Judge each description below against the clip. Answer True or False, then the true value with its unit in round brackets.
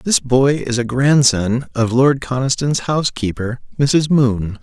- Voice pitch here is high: False (130 Hz)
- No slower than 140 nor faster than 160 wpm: True (145 wpm)